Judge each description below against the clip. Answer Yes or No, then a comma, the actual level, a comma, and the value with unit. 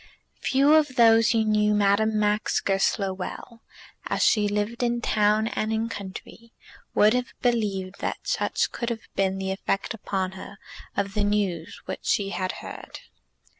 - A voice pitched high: Yes, high, 210 Hz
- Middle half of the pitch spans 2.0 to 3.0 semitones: Yes, narrow, 2.6 semitones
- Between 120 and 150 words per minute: No, average, 160 wpm